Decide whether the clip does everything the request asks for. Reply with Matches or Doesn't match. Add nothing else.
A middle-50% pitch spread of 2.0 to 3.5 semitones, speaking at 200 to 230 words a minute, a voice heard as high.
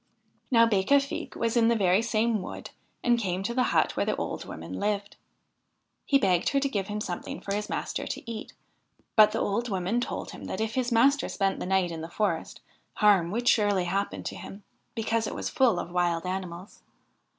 Doesn't match